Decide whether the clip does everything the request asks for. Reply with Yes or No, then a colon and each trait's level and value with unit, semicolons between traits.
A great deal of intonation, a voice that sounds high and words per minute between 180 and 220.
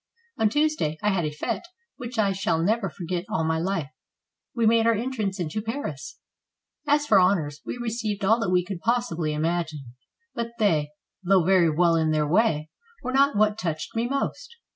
Yes: wide, 6.0 semitones; high, 195 Hz; average, 185 wpm